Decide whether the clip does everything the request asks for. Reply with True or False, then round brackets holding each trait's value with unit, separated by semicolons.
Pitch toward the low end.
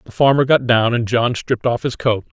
True (120 Hz)